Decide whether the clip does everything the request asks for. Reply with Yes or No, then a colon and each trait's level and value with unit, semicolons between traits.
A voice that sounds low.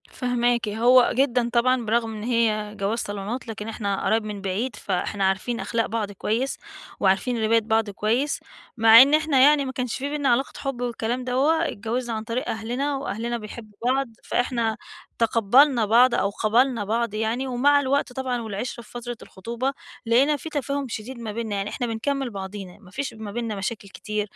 No: high, 235 Hz